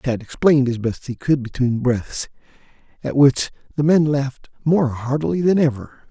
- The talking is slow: No, average, 165 wpm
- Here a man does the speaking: Yes, male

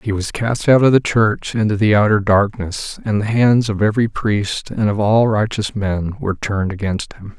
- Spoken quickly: Yes, fast, 210 wpm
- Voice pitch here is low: Yes, low, 105 Hz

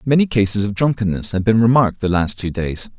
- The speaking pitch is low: Yes, low, 105 Hz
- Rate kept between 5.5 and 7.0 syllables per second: Yes, 6.0 syllables/s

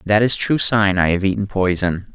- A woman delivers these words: No, male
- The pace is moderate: No, fast, 225 wpm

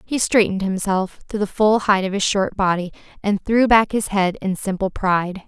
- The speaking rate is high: Yes, fast, 210 wpm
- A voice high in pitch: Yes, high, 200 Hz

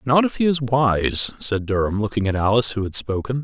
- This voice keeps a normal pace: No, fast, 225 wpm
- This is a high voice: No, low, 115 Hz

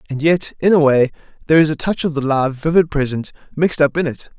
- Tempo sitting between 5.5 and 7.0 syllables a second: Yes, 6.4 syllables/s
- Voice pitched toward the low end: No, medium, 150 Hz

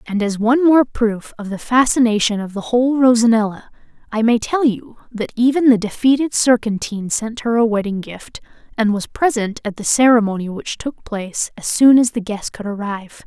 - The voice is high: Yes, high, 230 Hz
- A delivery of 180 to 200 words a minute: Yes, average, 190 wpm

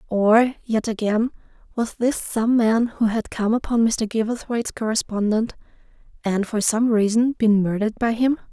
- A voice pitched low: No, high, 225 Hz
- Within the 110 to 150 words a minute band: Yes, average, 140 wpm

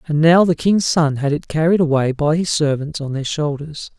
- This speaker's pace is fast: Yes, fast, 225 wpm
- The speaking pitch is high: No, medium, 155 Hz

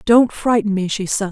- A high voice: Yes, high, 210 Hz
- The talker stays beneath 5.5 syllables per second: Yes, 5.0 syllables/s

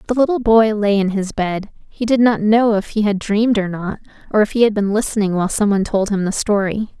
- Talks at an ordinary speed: No, fast, 250 wpm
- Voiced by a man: No, female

